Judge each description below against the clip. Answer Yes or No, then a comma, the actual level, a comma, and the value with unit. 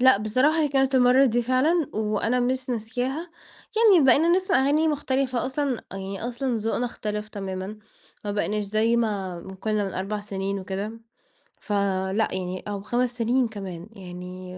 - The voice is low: No, high, 220 Hz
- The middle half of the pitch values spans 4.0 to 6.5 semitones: Yes, average, 4.7 semitones